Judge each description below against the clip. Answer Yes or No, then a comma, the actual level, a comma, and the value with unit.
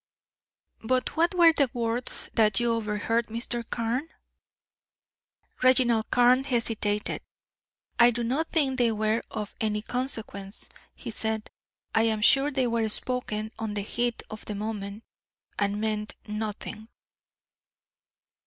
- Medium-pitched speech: No, high, 225 Hz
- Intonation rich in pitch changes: No, average, 2.7 semitones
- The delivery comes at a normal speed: No, slow, 125 wpm